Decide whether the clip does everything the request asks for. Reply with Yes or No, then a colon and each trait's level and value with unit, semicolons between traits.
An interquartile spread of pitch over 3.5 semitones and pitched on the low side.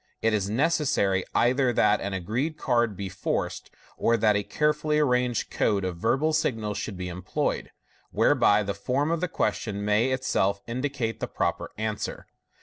Yes: average, 4.6 semitones; low, 115 Hz